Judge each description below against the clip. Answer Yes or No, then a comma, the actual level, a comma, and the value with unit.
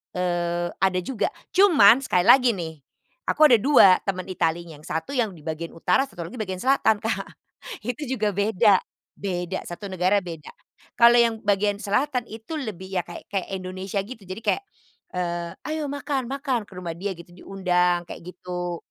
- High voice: Yes, high, 195 Hz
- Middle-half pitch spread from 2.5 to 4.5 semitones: No, average, 5.1 semitones